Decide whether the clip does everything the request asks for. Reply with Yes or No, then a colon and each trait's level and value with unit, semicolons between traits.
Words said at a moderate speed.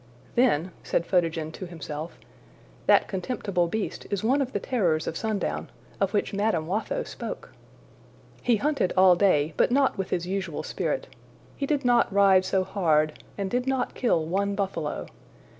Yes: average, 160 wpm